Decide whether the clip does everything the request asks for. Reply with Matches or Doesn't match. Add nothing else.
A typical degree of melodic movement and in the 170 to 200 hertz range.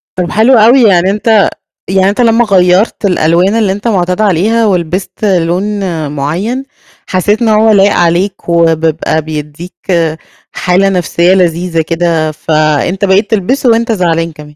Matches